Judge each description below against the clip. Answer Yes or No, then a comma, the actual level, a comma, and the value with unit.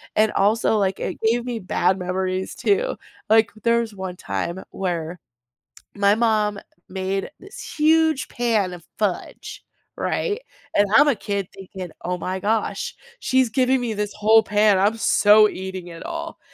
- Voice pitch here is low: No, high, 210 Hz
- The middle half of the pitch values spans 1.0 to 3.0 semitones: No, average, 3.7 semitones